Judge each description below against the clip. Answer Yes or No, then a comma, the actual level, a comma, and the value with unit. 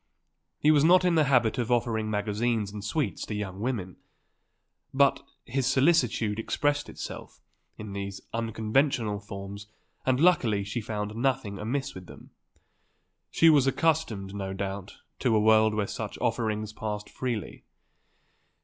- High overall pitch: No, low, 110 Hz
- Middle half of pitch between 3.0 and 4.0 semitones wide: No, average, 4.6 semitones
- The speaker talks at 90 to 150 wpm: Yes, average, 140 wpm